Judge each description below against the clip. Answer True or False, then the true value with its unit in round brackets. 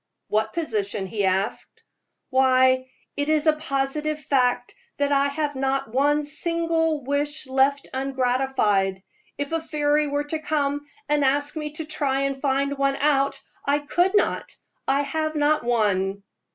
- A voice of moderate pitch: False (280 Hz)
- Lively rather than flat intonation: False (2.4 semitones)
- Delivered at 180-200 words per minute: False (150 wpm)